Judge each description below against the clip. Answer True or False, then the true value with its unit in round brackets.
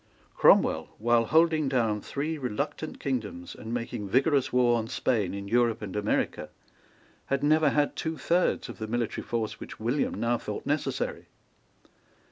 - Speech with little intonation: False (4.5 semitones)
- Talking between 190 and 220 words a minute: False (150 wpm)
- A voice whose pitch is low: True (120 Hz)